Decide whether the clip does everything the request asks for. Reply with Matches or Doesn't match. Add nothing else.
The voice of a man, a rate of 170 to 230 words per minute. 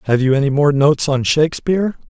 Matches